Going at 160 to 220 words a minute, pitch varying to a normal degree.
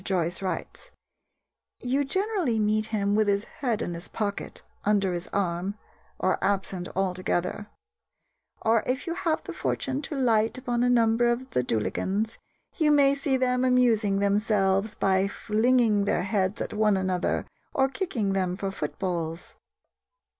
No: average, 145 wpm; average, 4.6 semitones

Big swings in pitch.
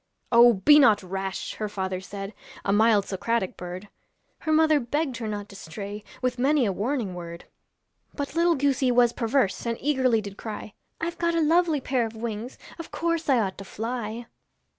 Yes: wide, 5.7 semitones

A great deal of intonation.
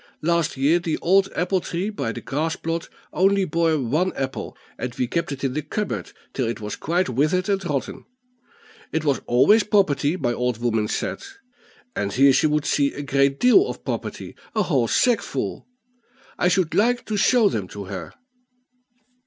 Yes: wide, 5.8 semitones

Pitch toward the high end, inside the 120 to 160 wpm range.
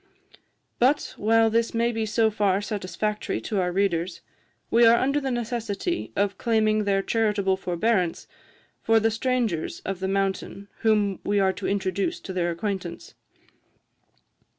Yes: high, 210 Hz; average, 145 wpm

